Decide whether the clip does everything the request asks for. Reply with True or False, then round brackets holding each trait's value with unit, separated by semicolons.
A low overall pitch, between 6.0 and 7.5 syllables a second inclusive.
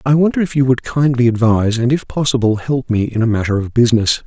True (125 Hz; 6.2 syllables/s)